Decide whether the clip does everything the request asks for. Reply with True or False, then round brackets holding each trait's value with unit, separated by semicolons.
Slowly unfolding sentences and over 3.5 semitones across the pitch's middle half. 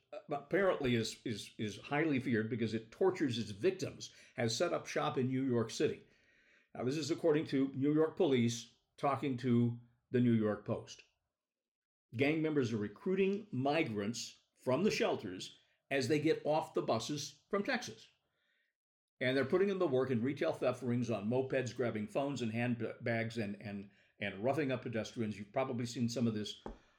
False (175 wpm; 4.1 semitones)